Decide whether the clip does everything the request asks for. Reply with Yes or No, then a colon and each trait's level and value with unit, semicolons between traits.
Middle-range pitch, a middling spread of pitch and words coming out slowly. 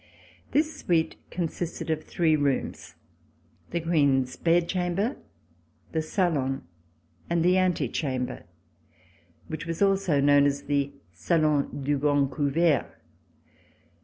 Yes: medium, 155 Hz; average, 3.5 semitones; slow, 110 wpm